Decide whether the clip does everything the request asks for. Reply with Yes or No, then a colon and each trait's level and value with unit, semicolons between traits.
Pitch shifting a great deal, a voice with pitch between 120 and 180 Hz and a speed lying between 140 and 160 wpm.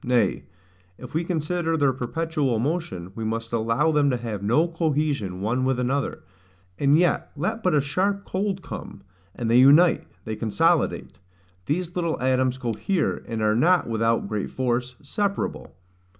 Yes: wide, 6.1 semitones; low, 135 Hz; average, 155 wpm